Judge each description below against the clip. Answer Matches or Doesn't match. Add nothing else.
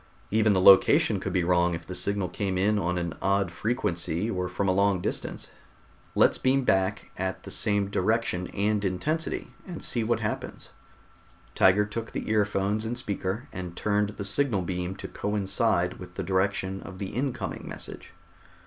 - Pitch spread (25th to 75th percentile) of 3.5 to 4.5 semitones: Doesn't match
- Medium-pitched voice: Doesn't match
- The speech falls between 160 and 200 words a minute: Matches